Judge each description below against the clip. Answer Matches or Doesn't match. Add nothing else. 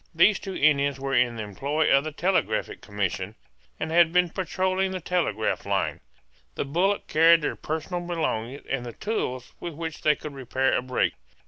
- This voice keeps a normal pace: Matches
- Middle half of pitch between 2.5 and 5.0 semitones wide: Doesn't match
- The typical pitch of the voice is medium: Matches